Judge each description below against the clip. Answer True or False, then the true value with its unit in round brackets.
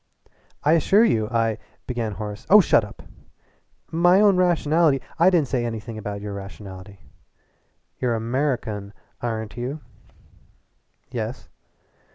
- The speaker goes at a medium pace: False (130 wpm)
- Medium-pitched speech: False (120 Hz)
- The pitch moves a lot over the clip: True (6.9 semitones)